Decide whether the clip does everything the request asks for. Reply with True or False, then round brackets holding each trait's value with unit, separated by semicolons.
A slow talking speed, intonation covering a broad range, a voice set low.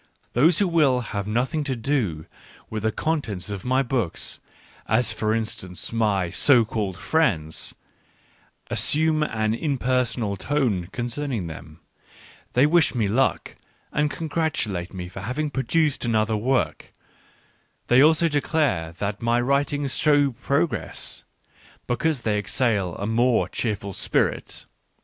True (130 wpm; 5.7 semitones; 120 Hz)